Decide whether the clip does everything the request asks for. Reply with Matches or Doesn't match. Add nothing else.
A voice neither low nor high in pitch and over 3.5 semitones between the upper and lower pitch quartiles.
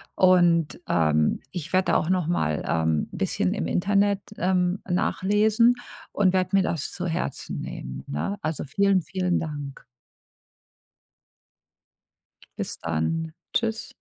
Matches